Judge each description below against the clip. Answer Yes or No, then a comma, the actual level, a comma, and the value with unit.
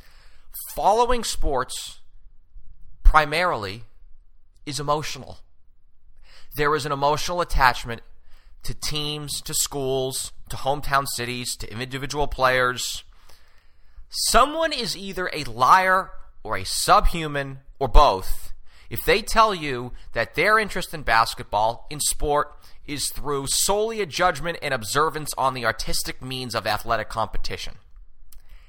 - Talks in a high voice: No, low, 125 Hz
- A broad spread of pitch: Yes, wide, 8.2 semitones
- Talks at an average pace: No, slow, 115 wpm